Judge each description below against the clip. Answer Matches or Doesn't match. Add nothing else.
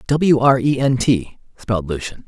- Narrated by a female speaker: Doesn't match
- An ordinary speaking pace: Matches